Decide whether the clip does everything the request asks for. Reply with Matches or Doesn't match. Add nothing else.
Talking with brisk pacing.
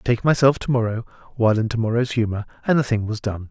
Matches